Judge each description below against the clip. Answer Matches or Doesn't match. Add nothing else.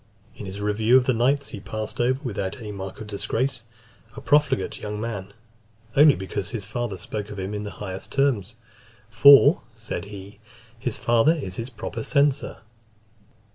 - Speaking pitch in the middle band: Doesn't match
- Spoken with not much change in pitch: Doesn't match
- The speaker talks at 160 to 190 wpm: Matches